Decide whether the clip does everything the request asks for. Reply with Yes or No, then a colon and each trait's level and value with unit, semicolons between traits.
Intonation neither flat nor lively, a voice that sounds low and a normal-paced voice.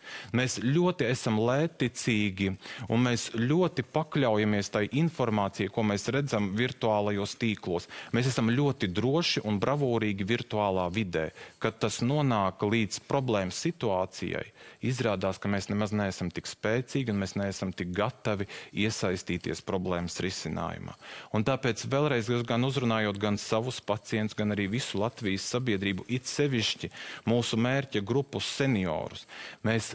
No: average, 3.7 semitones; low, 110 Hz; slow, 120 wpm